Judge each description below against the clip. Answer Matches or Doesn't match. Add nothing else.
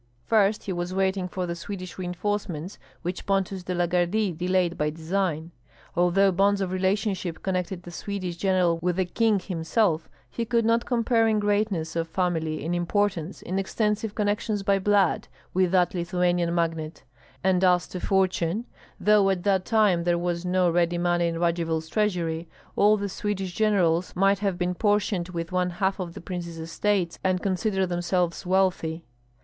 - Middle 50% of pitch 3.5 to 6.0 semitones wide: Doesn't match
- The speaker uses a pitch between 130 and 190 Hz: Matches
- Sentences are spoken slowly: Doesn't match